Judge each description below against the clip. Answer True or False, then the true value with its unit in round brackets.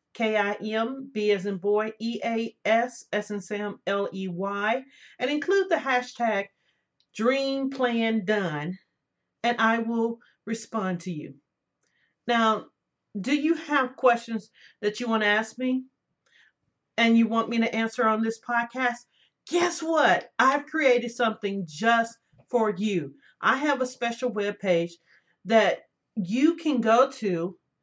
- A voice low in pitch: False (225 Hz)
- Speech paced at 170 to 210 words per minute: False (145 wpm)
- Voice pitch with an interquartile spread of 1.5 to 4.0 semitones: True (3.4 semitones)